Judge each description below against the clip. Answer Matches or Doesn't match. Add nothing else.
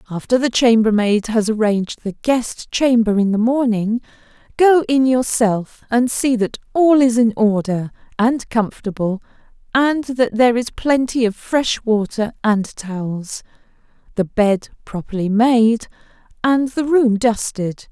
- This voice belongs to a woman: Matches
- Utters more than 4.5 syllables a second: Doesn't match